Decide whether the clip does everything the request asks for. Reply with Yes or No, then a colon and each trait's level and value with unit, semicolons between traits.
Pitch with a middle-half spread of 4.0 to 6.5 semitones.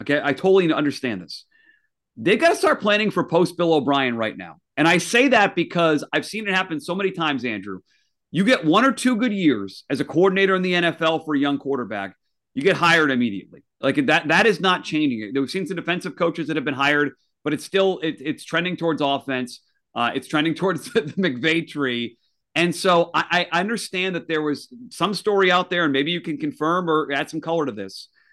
Yes: average, 4.9 semitones